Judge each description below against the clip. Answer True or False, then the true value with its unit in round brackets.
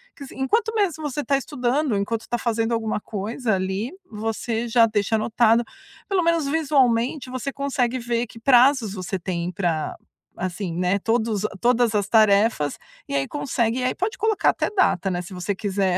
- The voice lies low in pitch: False (230 Hz)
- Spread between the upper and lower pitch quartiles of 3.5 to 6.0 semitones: True (4.8 semitones)